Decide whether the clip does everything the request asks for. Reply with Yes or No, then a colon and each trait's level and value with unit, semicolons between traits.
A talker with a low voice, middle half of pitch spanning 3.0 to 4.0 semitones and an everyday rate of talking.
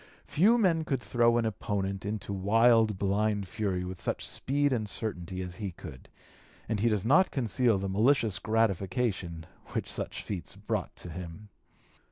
Yes: low, 105 Hz; average, 3.7 semitones; average, 160 wpm